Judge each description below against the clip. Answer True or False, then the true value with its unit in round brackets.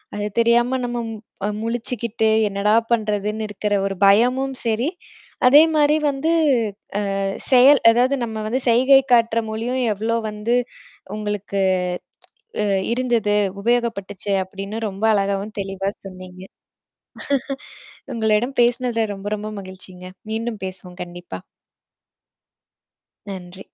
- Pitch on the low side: False (220 Hz)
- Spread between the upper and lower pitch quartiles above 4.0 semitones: False (3.4 semitones)